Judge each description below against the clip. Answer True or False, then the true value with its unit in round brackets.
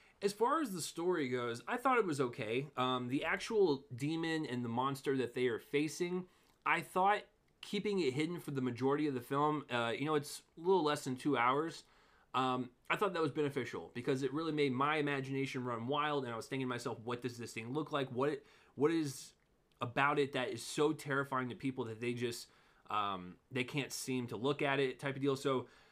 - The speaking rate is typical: False (220 wpm)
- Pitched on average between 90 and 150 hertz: True (140 Hz)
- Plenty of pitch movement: False (3.3 semitones)